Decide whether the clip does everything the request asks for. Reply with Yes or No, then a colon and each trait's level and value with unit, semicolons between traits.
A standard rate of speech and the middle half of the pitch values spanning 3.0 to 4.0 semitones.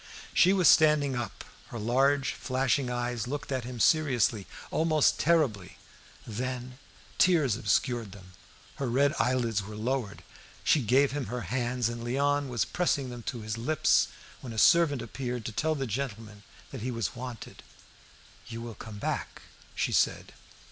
Yes: average, 155 wpm; average, 3.4 semitones